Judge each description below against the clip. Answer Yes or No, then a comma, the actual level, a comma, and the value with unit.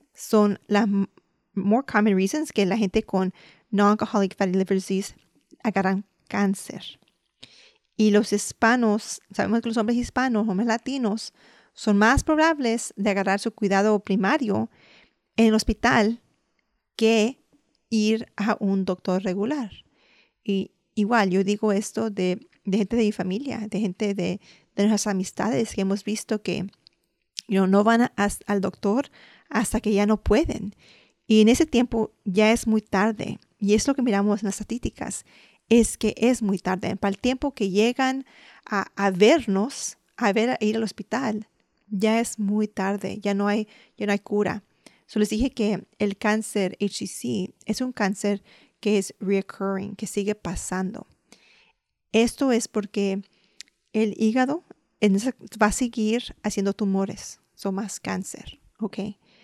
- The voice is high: Yes, high, 210 Hz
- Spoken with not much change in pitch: Yes, narrow, 2.2 semitones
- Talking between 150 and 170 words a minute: Yes, average, 155 wpm